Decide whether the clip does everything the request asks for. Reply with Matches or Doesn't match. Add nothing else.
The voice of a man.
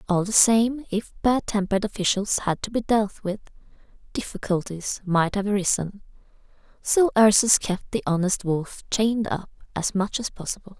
Doesn't match